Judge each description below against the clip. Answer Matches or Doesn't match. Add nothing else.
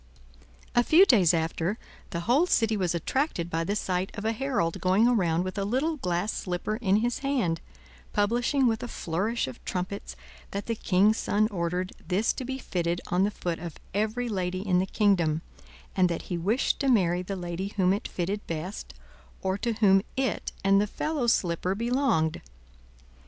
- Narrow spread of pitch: Doesn't match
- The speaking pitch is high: Matches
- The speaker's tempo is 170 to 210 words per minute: Matches